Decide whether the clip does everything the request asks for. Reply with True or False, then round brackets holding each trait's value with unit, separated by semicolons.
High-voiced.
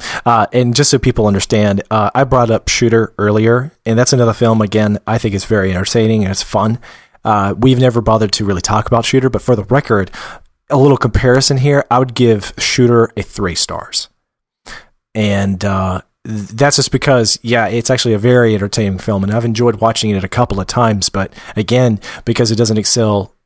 False (115 Hz)